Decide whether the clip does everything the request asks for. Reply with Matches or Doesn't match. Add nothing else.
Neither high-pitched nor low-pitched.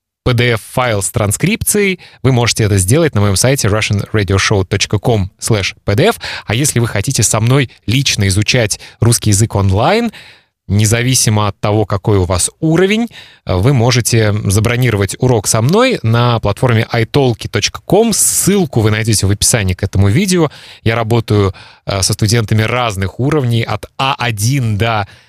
Doesn't match